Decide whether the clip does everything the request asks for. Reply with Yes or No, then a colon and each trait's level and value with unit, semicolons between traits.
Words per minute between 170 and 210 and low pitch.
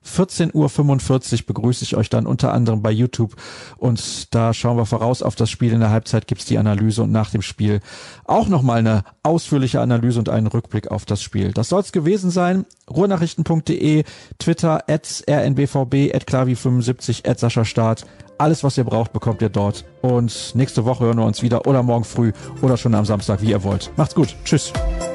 Yes: average, 185 wpm; low, 120 Hz